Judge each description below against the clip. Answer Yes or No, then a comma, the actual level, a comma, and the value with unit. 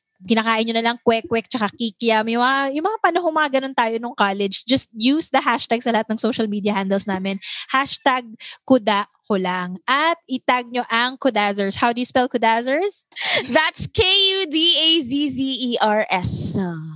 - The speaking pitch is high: Yes, high, 240 Hz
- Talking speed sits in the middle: Yes, average, 150 wpm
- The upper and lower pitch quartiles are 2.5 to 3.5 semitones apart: No, average, 4.0 semitones